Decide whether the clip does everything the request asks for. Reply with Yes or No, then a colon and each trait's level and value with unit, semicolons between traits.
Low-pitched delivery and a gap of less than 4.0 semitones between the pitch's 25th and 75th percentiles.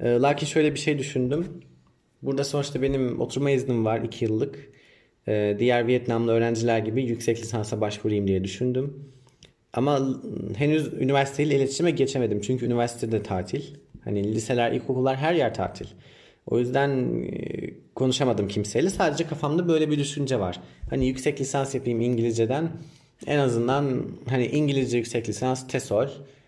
Yes: low, 130 Hz; average, 3.3 semitones